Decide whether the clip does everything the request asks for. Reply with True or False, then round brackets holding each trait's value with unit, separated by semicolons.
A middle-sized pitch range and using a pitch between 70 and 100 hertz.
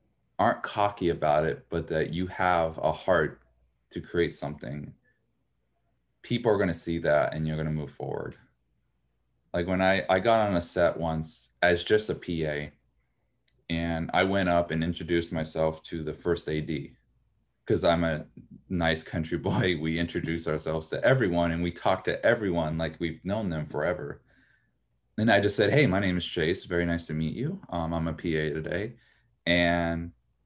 False (1.8 semitones; 85 Hz)